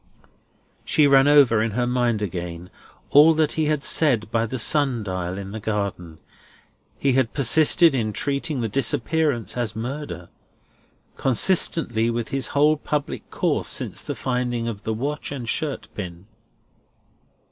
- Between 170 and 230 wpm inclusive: No, average, 145 wpm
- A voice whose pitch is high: No, low, 125 Hz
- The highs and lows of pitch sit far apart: No, average, 4.9 semitones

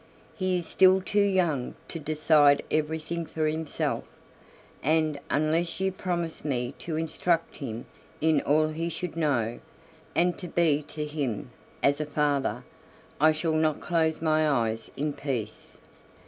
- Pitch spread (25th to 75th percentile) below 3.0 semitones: Yes, narrow, 2.4 semitones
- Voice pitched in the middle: Yes, medium, 155 Hz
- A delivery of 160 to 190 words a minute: No, average, 145 wpm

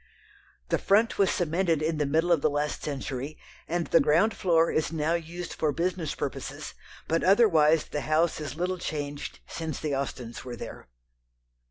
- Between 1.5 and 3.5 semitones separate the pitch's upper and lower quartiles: Yes, narrow, 2.6 semitones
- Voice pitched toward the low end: No, medium, 160 Hz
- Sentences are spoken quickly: No, average, 170 wpm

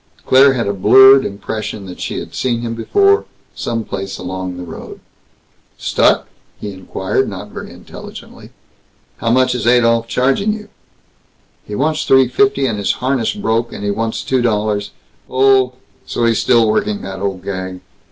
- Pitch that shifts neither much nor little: Yes, average, 4.5 semitones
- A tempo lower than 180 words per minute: Yes, average, 165 wpm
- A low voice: Yes, low, 115 Hz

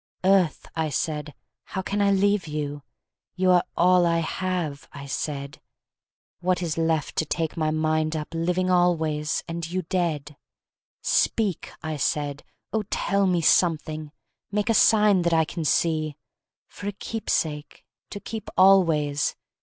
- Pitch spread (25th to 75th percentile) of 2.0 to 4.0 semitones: Yes, average, 3.3 semitones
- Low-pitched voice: No, medium, 165 Hz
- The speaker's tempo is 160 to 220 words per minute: No, average, 145 wpm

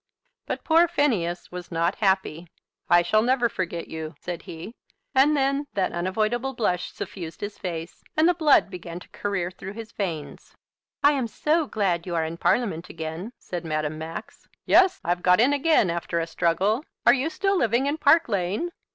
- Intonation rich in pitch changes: Yes, wide, 7.8 semitones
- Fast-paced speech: No, average, 180 wpm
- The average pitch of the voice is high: Yes, high, 195 Hz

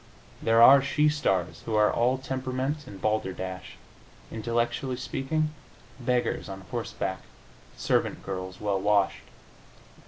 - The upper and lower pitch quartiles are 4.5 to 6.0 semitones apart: Yes, average, 5.2 semitones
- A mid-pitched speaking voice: No, low, 115 Hz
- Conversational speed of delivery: No, slow, 115 wpm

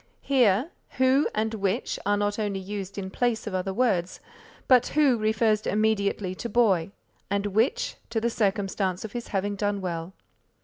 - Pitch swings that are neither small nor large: Yes, average, 3.1 semitones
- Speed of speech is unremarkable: Yes, average, 165 wpm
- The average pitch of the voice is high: Yes, high, 205 Hz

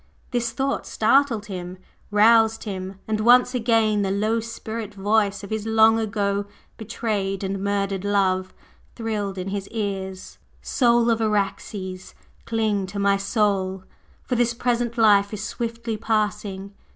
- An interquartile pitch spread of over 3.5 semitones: No, narrow, 2.4 semitones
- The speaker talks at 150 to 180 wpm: No, average, 140 wpm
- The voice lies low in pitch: No, high, 210 Hz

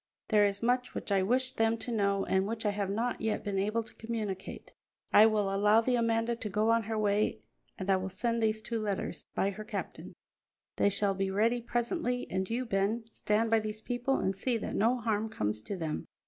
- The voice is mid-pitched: No, high, 215 Hz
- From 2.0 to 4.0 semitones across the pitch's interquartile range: Yes, narrow, 2.6 semitones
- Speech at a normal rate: No, fast, 215 wpm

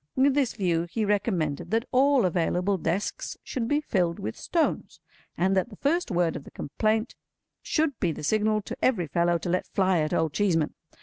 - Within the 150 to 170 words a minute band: No, average, 190 wpm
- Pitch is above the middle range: Yes, high, 195 Hz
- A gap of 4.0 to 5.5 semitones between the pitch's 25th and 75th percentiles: Yes, average, 5.2 semitones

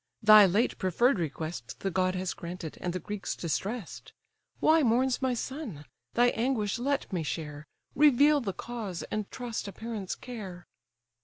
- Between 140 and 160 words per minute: Yes, average, 155 wpm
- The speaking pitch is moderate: No, high, 210 Hz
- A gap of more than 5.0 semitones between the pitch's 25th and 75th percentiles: Yes, wide, 5.4 semitones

